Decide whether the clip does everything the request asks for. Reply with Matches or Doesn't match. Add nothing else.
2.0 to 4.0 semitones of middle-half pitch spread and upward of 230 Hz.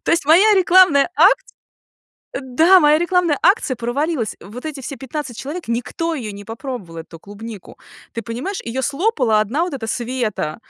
Doesn't match